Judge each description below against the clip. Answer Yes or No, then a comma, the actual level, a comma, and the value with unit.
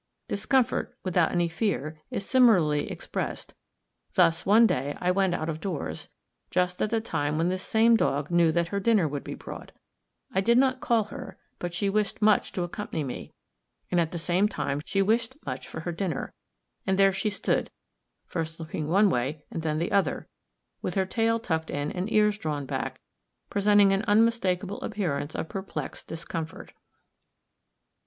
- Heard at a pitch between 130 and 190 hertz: Yes, medium, 185 Hz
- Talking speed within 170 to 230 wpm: Yes, average, 175 wpm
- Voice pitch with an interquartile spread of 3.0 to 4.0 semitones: No, average, 4.5 semitones